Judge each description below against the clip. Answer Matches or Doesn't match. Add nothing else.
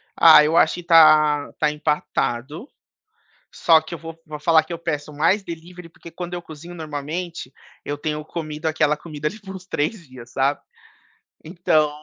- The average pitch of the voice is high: Doesn't match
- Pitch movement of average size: Doesn't match